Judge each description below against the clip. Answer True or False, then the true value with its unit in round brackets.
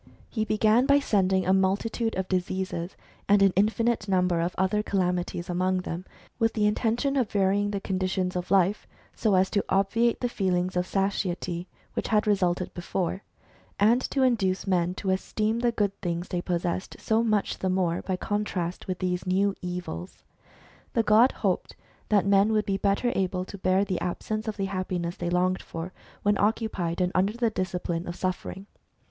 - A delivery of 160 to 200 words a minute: True (180 wpm)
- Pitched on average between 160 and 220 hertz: True (190 Hz)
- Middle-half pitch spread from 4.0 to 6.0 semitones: False (2.6 semitones)